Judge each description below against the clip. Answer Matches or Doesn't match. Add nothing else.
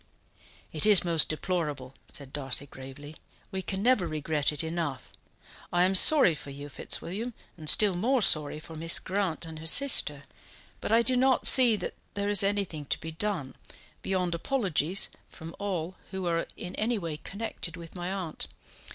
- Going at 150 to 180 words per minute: Matches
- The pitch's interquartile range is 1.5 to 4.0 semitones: Doesn't match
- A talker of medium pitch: Matches